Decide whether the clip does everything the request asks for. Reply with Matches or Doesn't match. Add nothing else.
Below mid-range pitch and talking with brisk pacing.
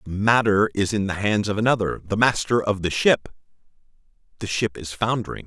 Doesn't match